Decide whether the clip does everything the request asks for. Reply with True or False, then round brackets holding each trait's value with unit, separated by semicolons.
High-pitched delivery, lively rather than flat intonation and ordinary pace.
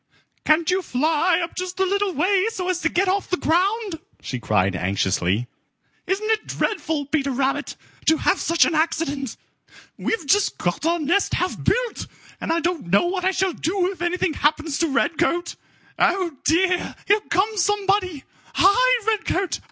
False (350 Hz; 3.9 semitones; 165 wpm)